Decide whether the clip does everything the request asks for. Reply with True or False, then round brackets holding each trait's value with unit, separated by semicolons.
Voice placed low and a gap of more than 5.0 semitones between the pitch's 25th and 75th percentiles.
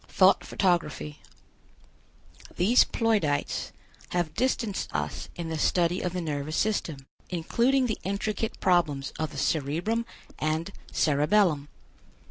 False (175 Hz; 5.5 semitones)